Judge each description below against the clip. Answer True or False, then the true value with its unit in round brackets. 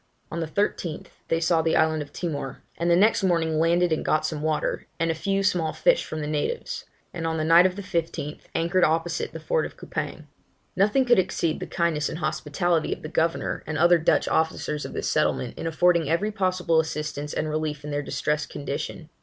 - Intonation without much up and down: True (2.2 semitones)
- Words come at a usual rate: False (210 wpm)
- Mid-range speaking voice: True (165 Hz)